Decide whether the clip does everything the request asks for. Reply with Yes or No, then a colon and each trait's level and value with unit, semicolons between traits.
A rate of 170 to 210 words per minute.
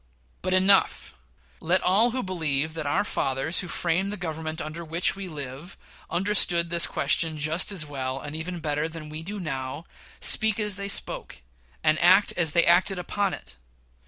Yes: average, 175 wpm